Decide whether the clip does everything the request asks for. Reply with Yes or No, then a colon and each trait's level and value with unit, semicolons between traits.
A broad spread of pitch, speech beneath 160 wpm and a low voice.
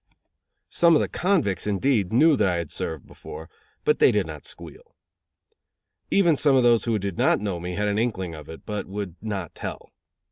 No: wide, 6.8 semitones; average, 200 wpm; low, 105 Hz